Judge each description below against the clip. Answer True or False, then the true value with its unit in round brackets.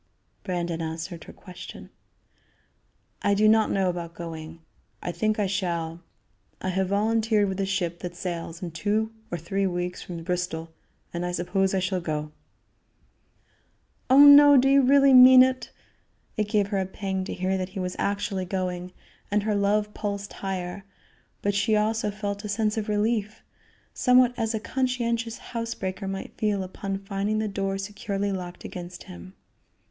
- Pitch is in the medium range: False (195 Hz)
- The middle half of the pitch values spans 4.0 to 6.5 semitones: False (3.1 semitones)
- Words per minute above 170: False (165 wpm)